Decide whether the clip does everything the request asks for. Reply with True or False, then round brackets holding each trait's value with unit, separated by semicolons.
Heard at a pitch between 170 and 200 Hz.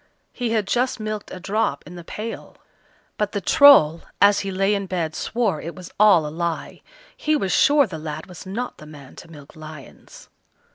True (185 Hz)